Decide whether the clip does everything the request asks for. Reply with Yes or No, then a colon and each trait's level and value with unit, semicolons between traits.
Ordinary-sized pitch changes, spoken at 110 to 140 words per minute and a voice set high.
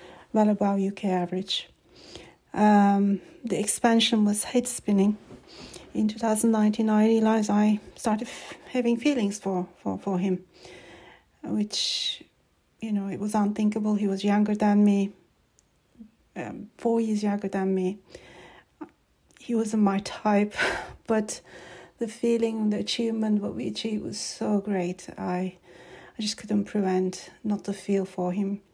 No: narrow, 2.2 semitones; slow, 135 wpm; high, 210 Hz